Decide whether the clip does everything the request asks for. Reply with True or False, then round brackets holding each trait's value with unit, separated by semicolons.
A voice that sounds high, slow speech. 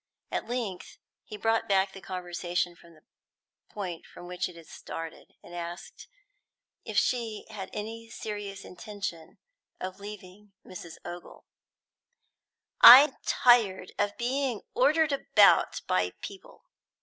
True (200 Hz; 125 wpm)